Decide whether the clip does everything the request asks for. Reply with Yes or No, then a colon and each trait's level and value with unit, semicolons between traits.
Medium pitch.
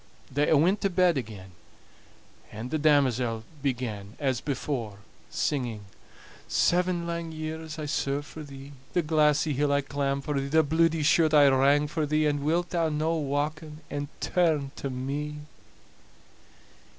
Yes: medium, 145 Hz